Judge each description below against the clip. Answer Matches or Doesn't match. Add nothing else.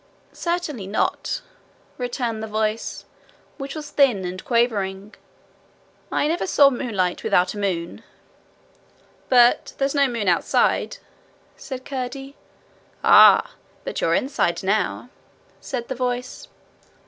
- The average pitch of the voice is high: Matches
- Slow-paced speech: Matches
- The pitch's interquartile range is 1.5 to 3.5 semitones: Doesn't match